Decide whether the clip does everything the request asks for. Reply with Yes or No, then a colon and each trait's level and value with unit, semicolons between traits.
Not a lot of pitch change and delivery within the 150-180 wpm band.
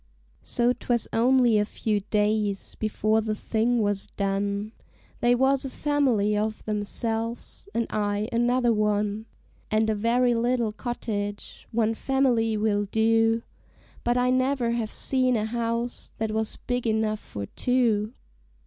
No: narrow, 2.3 semitones; average, 140 wpm